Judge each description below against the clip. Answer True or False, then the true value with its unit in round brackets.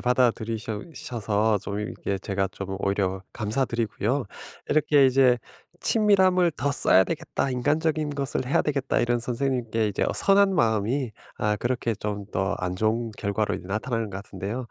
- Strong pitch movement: False (4.8 semitones)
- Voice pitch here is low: True (115 Hz)